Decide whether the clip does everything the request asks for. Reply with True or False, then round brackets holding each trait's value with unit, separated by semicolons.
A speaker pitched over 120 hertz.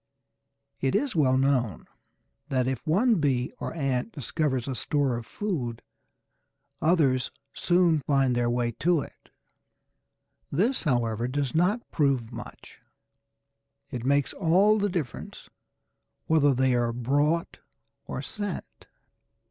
True (140 Hz)